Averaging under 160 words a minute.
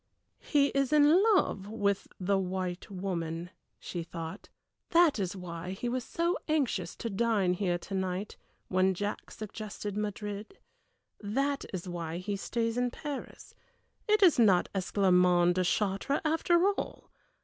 Yes: average, 140 wpm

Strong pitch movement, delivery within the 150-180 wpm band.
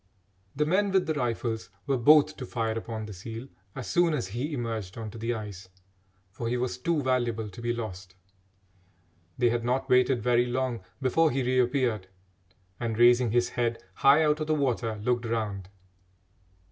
No: average, 2.9 semitones; average, 175 wpm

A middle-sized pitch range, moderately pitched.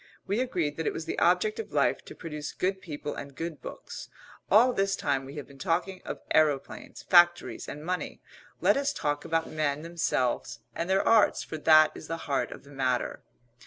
Yes: average, 4.2 semitones; medium, 160 Hz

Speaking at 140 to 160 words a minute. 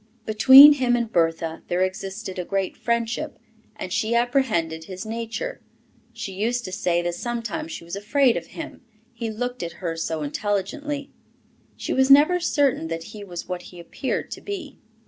No: average, 170 wpm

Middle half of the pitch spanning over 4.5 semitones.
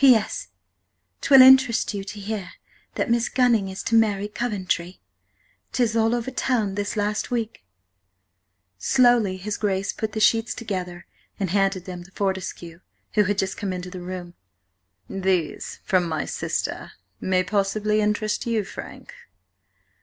No: average, 3.2 semitones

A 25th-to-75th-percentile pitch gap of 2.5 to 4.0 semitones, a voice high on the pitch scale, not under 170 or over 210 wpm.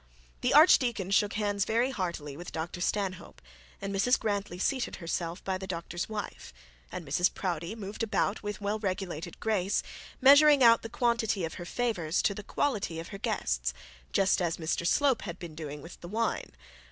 No: average, 4.4 semitones; high, 195 Hz; average, 175 wpm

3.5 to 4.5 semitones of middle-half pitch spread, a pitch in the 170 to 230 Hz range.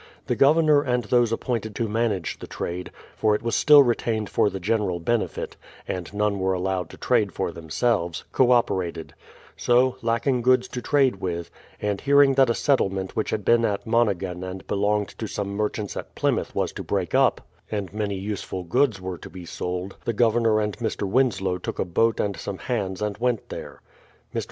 No: average, 4.0 semitones; low, 105 Hz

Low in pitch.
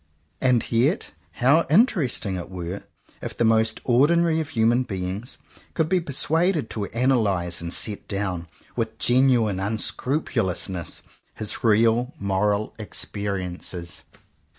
Yes: low, 110 Hz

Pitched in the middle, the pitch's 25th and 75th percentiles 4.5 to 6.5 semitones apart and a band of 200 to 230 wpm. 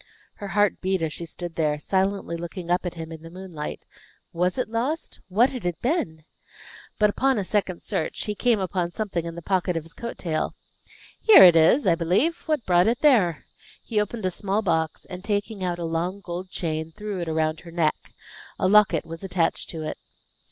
No: medium, 180 Hz; average, 3.9 semitones; fast, 205 wpm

